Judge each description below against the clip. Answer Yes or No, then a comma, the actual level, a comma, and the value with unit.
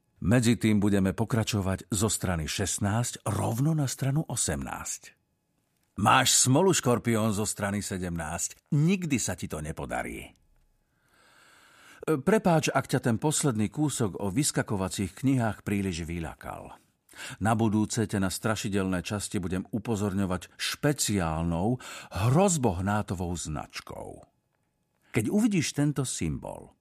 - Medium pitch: No, low, 110 Hz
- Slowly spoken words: Yes, slow, 105 wpm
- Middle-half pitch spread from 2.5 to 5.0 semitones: No, wide, 5.6 semitones